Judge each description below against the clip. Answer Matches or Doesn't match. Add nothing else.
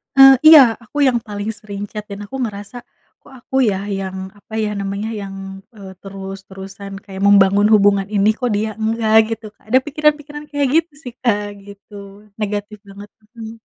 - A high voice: Matches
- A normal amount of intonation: Matches